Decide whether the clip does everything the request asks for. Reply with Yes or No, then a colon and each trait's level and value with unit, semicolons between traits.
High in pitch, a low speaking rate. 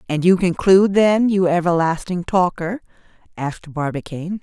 No: medium, 180 Hz; slow, 120 wpm